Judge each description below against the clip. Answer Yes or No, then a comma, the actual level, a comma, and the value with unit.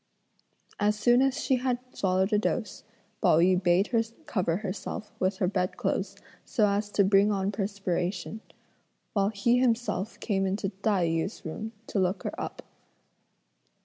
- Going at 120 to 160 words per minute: Yes, average, 155 wpm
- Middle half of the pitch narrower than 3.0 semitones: Yes, narrow, 2.4 semitones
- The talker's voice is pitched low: No, high, 200 Hz